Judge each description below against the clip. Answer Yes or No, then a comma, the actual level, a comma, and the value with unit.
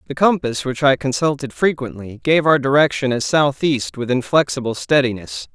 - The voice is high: No, low, 130 Hz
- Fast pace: No, average, 150 wpm